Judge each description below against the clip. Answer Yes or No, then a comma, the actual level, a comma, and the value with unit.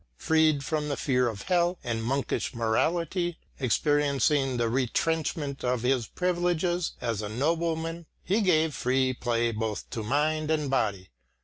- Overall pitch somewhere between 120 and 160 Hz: Yes, medium, 140 Hz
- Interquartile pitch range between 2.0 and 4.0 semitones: No, average, 5.1 semitones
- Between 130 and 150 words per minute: Yes, average, 140 wpm